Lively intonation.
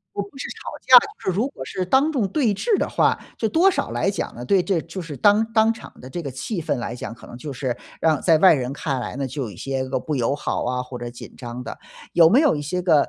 Yes: wide, 7.8 semitones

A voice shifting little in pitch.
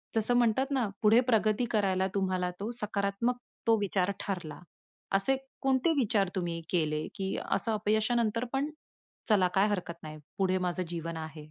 No: average, 4.0 semitones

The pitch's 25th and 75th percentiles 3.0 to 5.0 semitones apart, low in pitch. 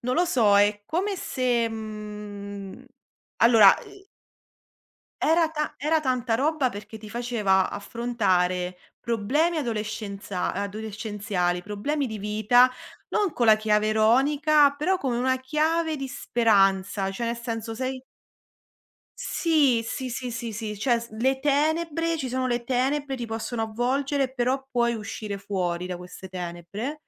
No: average, 4.5 semitones; high, 235 Hz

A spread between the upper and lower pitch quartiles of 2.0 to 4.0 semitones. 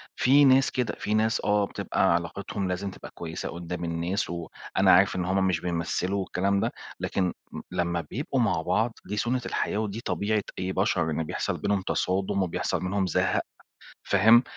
Yes: average, 2.9 semitones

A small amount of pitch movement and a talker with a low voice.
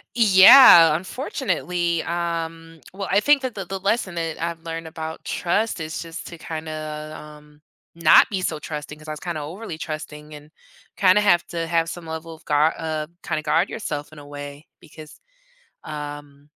No: narrow, 2.3 semitones; medium, 165 Hz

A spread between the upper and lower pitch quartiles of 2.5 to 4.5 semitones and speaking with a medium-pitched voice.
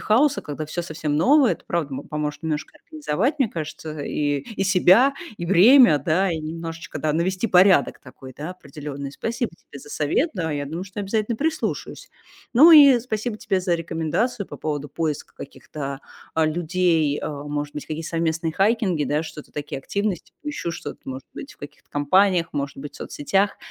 No: average, 5.3 semitones; medium, 165 Hz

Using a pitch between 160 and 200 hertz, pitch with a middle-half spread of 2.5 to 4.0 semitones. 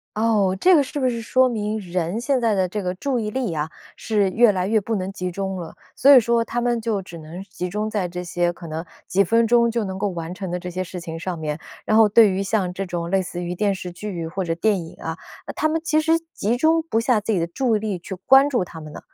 No: high, 195 Hz; average, 4.4 semitones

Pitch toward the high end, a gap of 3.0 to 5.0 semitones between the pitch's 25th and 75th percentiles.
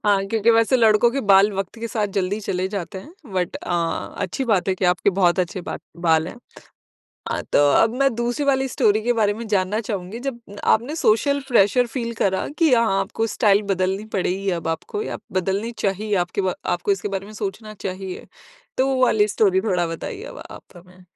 Yes: high, 205 Hz; average, 3.7 semitones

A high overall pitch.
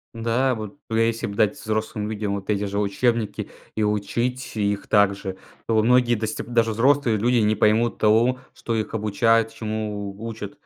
No: low, 110 Hz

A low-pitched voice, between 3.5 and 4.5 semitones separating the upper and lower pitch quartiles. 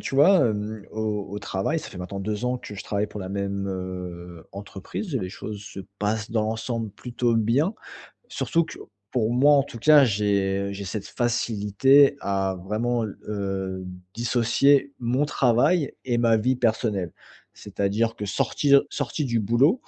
Yes: low, 110 Hz; average, 3.9 semitones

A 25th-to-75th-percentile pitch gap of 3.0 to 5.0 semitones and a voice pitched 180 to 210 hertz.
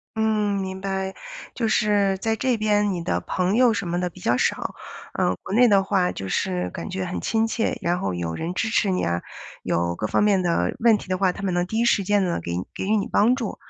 Yes: average, 3.5 semitones; high, 195 Hz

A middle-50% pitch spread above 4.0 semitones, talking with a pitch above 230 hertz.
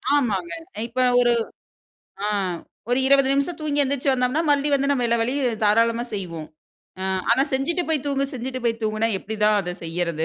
Yes: average, 4.4 semitones; high, 245 Hz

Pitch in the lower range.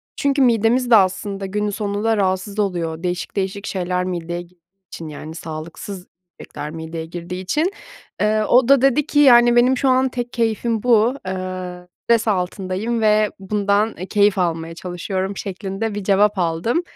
No: high, 200 Hz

